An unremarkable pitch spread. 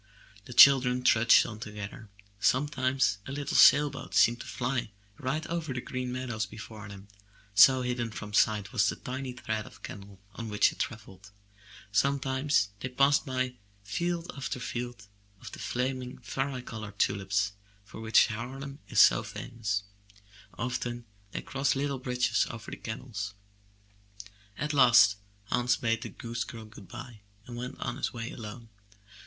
Yes: average, 3.4 semitones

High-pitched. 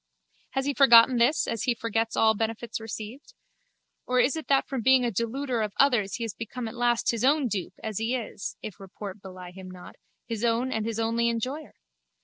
Yes: high, 230 Hz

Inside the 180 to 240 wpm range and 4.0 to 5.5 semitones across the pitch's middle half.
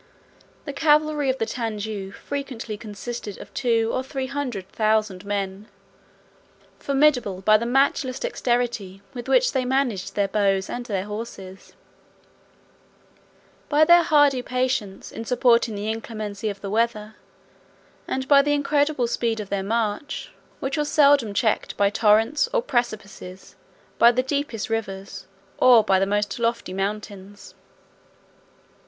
No: slow, 135 wpm; average, 4.5 semitones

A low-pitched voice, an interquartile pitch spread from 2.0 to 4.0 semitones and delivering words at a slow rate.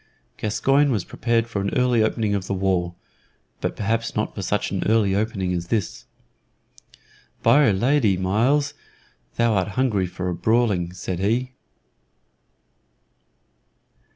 Yes: low, 105 Hz; average, 3.7 semitones; slow, 130 wpm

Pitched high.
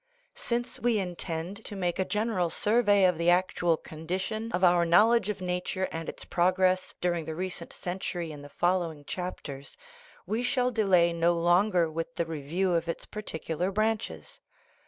No: medium, 180 Hz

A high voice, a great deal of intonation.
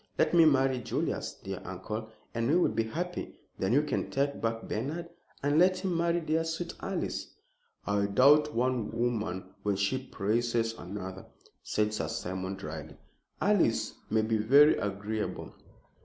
No: low, 115 Hz; wide, 6.5 semitones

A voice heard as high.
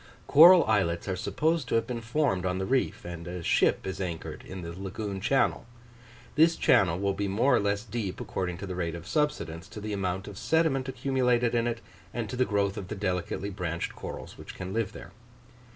No: low, 100 Hz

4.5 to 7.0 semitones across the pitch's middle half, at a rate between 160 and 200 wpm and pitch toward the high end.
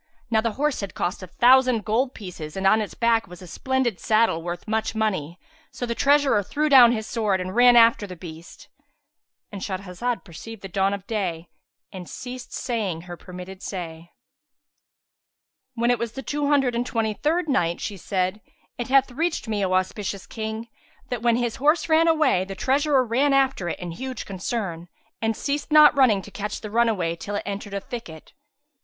Yes: average, 5.3 semitones; average, 185 wpm; high, 220 Hz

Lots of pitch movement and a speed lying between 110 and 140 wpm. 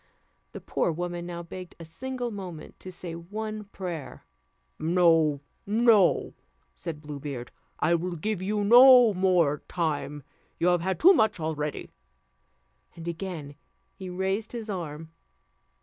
No: average, 4.1 semitones; slow, 135 wpm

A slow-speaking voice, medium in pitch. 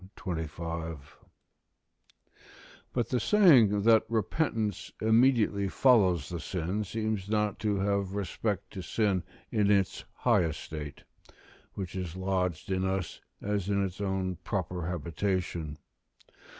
No: slow, 115 wpm; very low, 95 Hz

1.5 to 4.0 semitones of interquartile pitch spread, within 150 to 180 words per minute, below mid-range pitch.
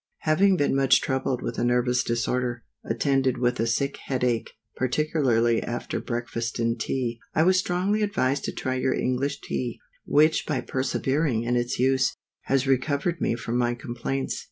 Yes: average, 2.7 semitones; average, 170 wpm; low, 130 Hz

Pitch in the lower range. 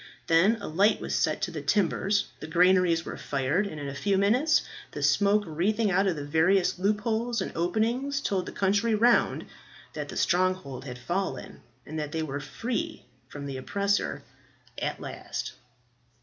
No: medium, 185 Hz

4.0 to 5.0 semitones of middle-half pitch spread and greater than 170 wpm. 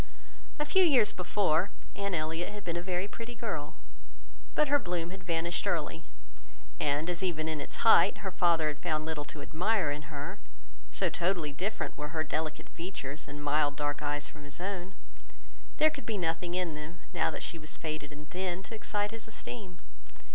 Yes: average, 4.3 semitones; average, 190 wpm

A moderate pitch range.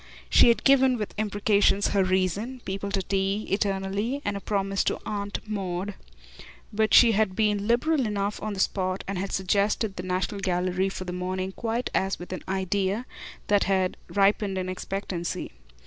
No: narrow, 1.9 semitones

